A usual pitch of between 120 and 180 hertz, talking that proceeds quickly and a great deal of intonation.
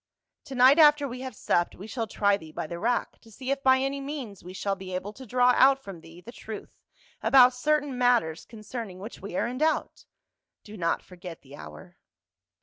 No: high, 230 Hz; fast, 210 wpm; wide, 5.9 semitones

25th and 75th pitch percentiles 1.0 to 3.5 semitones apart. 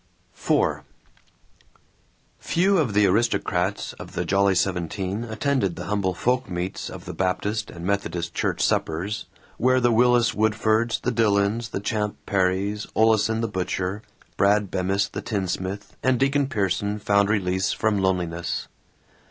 Yes: average, 3.1 semitones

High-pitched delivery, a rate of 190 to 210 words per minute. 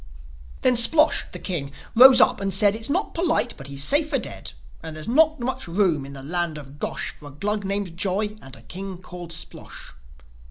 Yes: high, 195 Hz; average, 200 wpm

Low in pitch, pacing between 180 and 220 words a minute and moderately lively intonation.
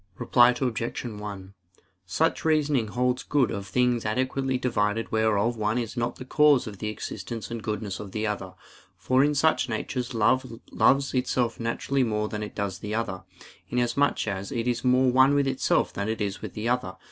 Yes: low, 115 Hz; average, 185 wpm; average, 3.4 semitones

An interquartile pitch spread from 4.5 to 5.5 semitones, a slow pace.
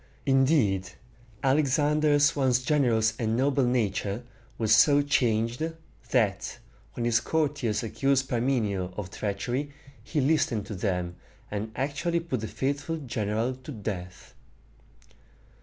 Yes: average, 5.0 semitones; slow, 115 wpm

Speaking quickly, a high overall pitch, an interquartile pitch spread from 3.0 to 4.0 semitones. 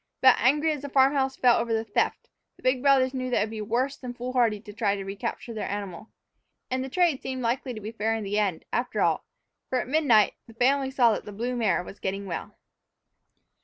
Yes: fast, 235 wpm; high, 240 Hz; average, 3.6 semitones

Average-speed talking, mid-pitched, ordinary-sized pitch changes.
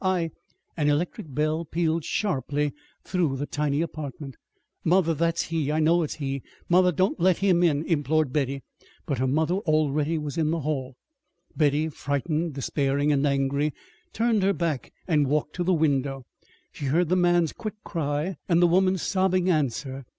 Yes: average, 170 wpm; medium, 155 Hz; average, 3.3 semitones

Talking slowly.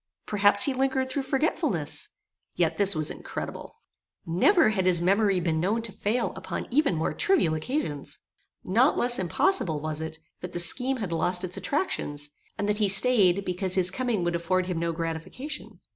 No: average, 175 wpm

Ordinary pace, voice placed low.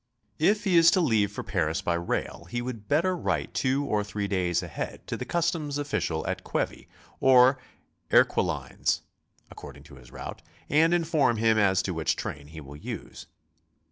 Yes: average, 170 wpm; low, 110 Hz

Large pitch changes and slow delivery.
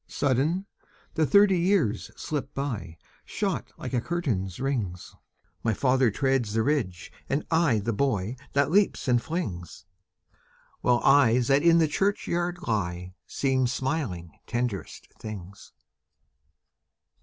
Yes: wide, 6.4 semitones; slow, 120 wpm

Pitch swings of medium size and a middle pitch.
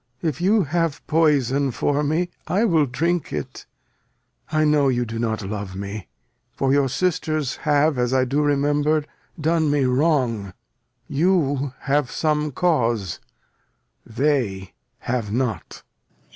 Yes: average, 4.1 semitones; medium, 145 Hz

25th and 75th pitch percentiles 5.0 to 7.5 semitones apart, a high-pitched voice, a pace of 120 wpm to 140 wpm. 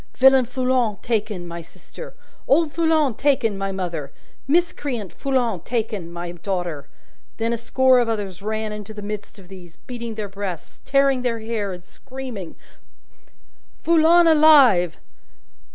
Yes: wide, 5.4 semitones; high, 225 Hz; slow, 135 wpm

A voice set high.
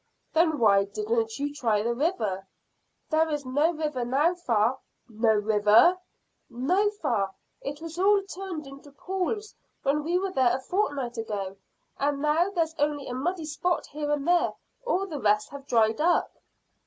Yes: very high, 290 Hz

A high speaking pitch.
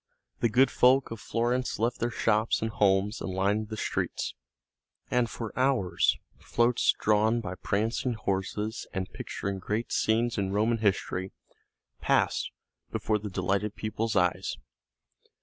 No: low, 110 Hz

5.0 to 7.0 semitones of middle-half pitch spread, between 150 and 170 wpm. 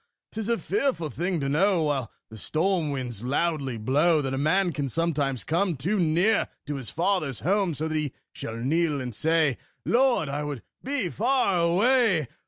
No: wide, 5.5 semitones; average, 180 wpm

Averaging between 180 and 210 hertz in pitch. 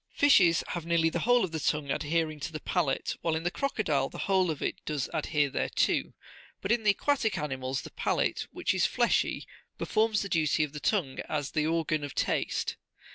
No: medium, 160 Hz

